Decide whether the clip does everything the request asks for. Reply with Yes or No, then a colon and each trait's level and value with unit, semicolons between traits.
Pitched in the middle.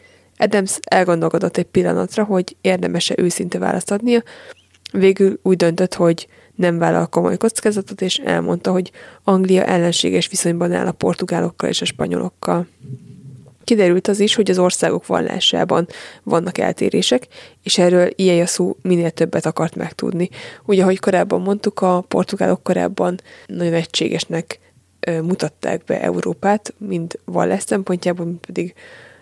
Yes: medium, 180 Hz